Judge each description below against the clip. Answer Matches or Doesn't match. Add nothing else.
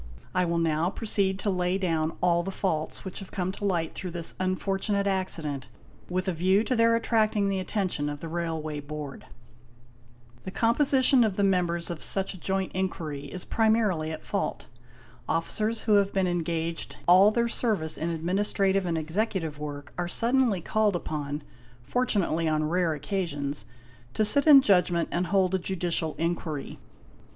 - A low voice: Doesn't match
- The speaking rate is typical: Matches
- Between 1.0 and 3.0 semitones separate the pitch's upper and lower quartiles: Doesn't match